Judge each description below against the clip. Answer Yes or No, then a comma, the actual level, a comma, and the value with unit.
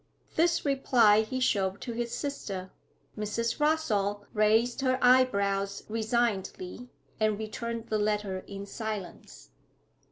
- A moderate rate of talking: No, slow, 115 wpm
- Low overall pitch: No, high, 220 Hz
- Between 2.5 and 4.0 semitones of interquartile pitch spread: Yes, average, 3.3 semitones